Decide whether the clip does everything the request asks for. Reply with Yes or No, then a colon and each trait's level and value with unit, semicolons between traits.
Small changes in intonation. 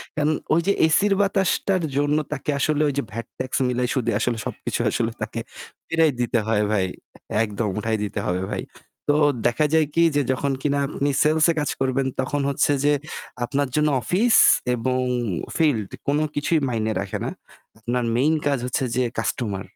No: average, 4.4 semitones